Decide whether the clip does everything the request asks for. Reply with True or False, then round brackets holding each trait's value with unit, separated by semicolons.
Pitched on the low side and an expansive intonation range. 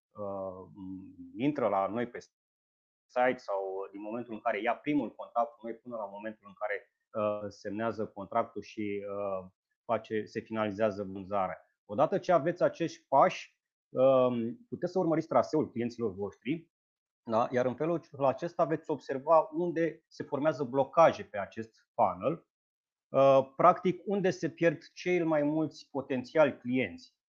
True (125 Hz; 7.1 semitones)